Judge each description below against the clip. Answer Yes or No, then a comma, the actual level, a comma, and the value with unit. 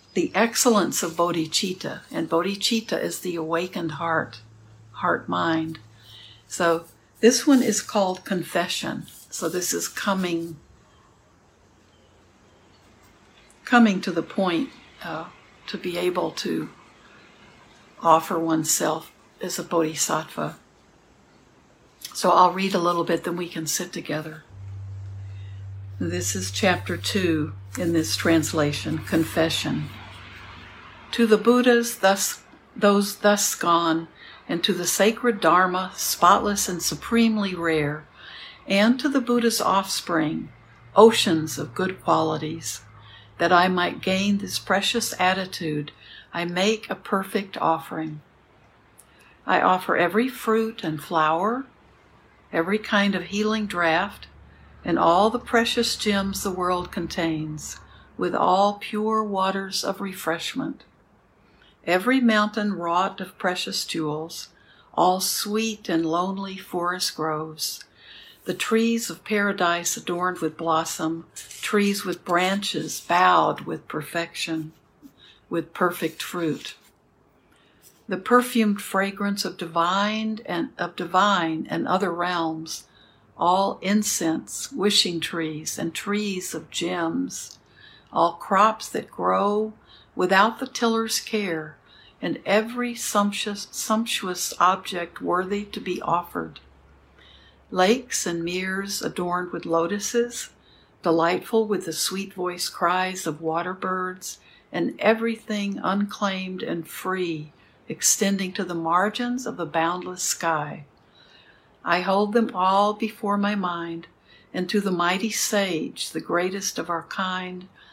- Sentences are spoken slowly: Yes, slow, 115 wpm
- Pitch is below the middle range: No, medium, 180 Hz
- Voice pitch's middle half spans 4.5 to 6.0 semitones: No, average, 4.1 semitones